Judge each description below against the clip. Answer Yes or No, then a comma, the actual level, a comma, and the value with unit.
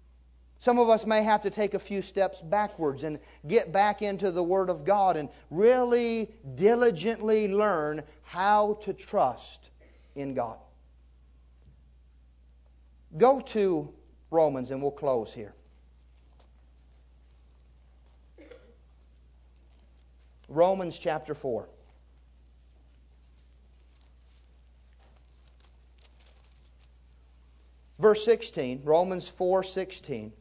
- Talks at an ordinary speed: No, slow, 85 wpm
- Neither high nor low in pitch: No, very low, 65 Hz